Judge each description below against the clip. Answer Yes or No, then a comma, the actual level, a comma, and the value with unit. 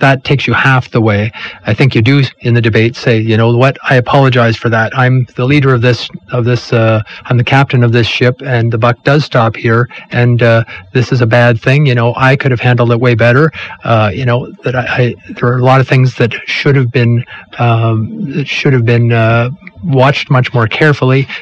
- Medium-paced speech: No, fast, 235 wpm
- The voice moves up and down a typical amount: No, narrow, 2.1 semitones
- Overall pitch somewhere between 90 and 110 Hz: No, low, 125 Hz